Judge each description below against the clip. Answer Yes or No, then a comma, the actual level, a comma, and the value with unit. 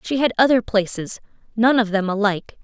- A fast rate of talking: No, average, 180 wpm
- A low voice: No, high, 220 Hz